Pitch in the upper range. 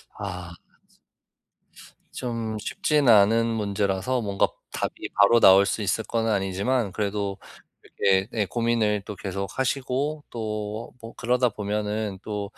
No: low, 105 Hz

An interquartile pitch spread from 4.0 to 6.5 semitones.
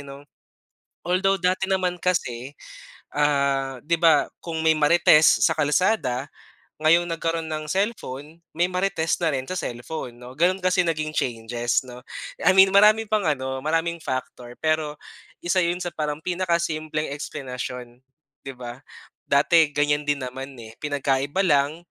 Yes: average, 4.5 semitones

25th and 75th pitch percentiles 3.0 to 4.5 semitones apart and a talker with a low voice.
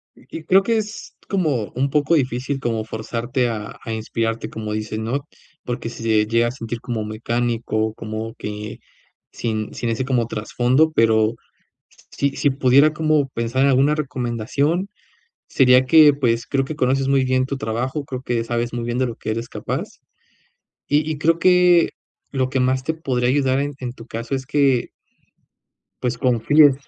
Yes: average, 3.5 semitones; low, 125 Hz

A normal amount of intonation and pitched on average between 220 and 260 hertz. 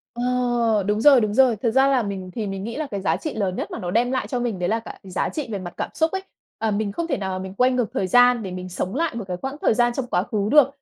Yes: average, 4.5 semitones; high, 225 Hz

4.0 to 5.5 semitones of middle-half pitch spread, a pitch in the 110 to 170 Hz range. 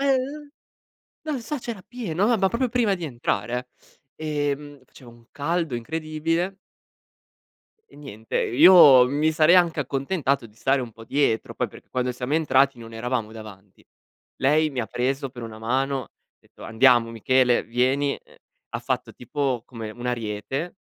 Yes: average, 5.1 semitones; low, 135 Hz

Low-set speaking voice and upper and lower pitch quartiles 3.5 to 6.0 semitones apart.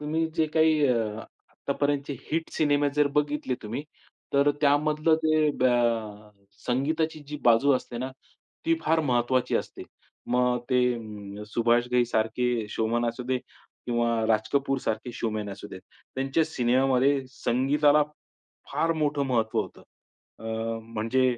Yes: low, 130 Hz; average, 4.0 semitones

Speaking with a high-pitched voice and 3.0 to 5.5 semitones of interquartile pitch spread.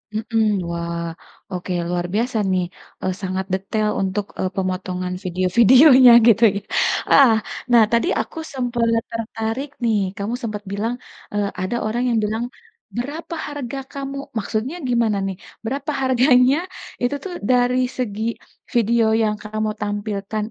Yes: high, 225 Hz; average, 3.8 semitones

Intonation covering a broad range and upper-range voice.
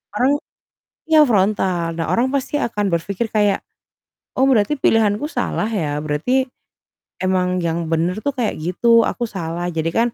Yes: wide, 5.9 semitones; high, 205 Hz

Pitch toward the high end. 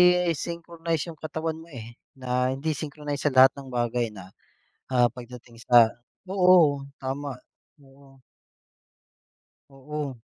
No: medium, 140 Hz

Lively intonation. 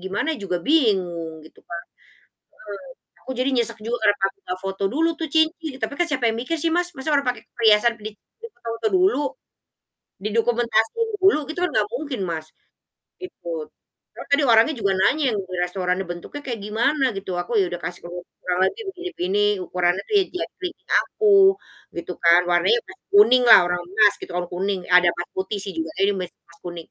Yes: wide, 8.4 semitones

